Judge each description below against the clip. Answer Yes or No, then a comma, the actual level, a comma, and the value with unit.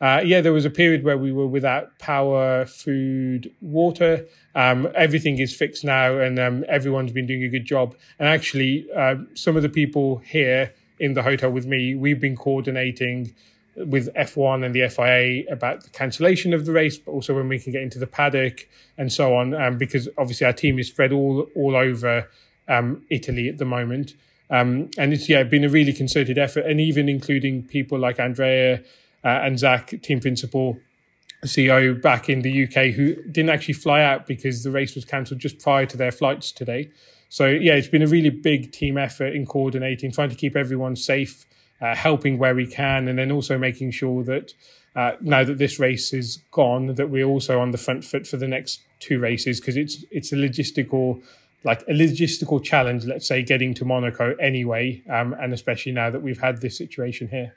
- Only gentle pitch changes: Yes, narrow, 2.0 semitones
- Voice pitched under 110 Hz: No, low, 135 Hz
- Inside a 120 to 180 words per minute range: No, average, 200 wpm